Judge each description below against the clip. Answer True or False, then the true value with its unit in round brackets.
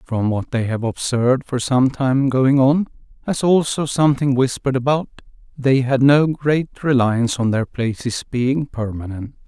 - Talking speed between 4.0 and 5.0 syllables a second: True (4.6 syllables/s)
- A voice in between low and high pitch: False (130 Hz)